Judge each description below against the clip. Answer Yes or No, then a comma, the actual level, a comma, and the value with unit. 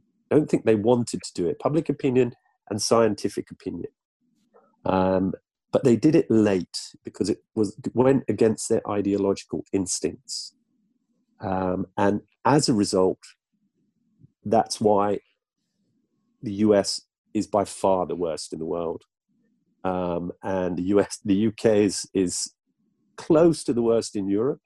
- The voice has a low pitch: Yes, low, 105 Hz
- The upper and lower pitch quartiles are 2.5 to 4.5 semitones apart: Yes, average, 3.8 semitones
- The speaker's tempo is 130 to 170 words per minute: Yes, average, 140 wpm